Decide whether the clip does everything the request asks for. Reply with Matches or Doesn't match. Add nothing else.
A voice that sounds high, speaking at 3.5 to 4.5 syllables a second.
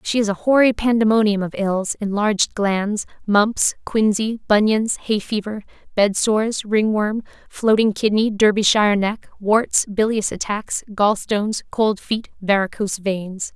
Matches